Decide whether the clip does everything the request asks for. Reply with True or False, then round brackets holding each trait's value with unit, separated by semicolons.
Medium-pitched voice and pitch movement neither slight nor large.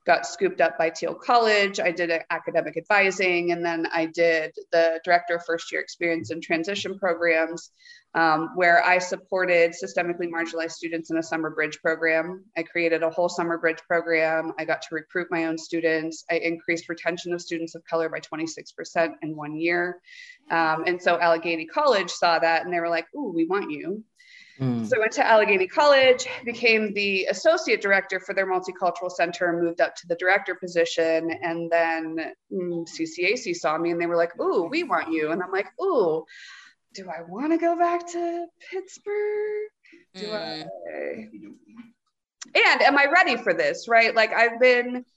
False (175 Hz; 5.9 semitones)